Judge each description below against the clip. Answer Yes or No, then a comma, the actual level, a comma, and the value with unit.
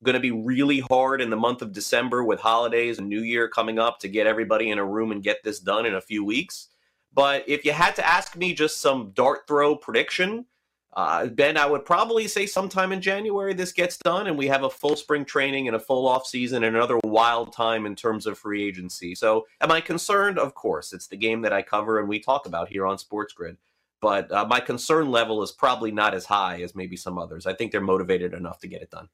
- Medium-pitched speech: No, low, 120 Hz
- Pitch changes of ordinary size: No, wide, 5.8 semitones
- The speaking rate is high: Yes, fast, 245 wpm